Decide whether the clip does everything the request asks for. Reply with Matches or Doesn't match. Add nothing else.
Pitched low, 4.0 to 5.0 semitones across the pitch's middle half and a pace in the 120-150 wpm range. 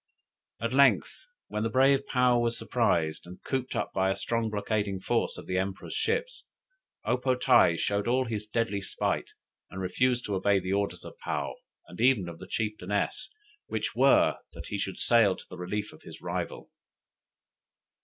Doesn't match